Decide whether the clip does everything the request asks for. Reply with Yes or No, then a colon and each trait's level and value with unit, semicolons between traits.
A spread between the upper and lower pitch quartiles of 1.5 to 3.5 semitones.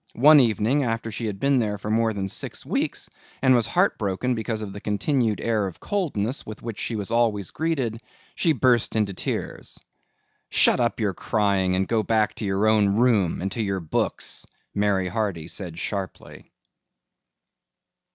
Yes: average, 3.1 semitones